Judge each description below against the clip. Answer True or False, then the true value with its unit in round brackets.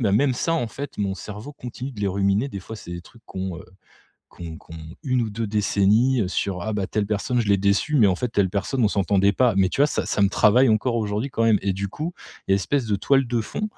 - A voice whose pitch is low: True (105 Hz)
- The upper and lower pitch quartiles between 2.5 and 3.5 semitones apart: False (4.0 semitones)